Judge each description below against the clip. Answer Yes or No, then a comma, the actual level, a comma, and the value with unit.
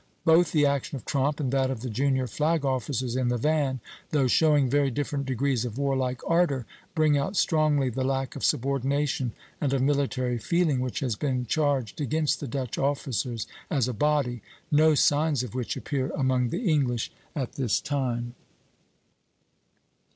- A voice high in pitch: No, low, 135 Hz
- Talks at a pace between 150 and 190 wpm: Yes, average, 165 wpm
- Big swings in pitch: No, narrow, 2.6 semitones